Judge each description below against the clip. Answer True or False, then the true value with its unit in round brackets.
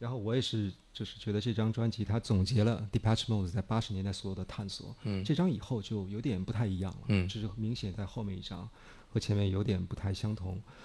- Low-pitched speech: True (110 Hz)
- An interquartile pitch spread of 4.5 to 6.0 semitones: False (2.5 semitones)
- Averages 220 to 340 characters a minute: False (385 characters per minute)